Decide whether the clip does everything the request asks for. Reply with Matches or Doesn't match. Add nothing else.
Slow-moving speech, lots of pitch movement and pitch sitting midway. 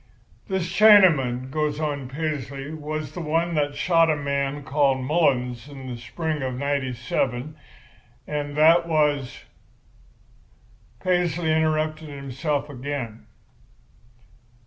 Doesn't match